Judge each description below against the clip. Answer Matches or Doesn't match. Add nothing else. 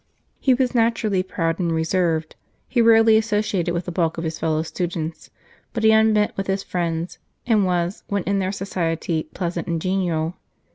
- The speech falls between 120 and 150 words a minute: Doesn't match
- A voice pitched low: Doesn't match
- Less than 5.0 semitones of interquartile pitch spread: Matches